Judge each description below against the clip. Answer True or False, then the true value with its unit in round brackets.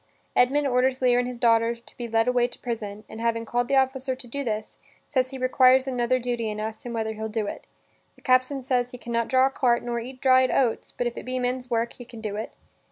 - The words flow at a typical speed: False (255 wpm)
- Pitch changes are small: True (1.9 semitones)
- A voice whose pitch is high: True (245 Hz)